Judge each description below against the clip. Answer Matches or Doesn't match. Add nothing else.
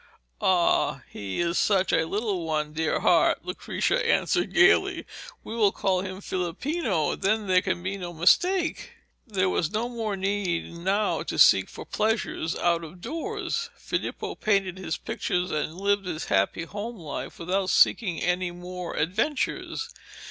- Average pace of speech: Matches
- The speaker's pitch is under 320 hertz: Matches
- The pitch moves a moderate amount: Matches